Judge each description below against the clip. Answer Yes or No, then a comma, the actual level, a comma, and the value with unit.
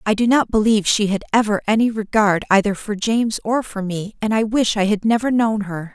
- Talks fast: Yes, fast, 230 wpm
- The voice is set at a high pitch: Yes, high, 215 Hz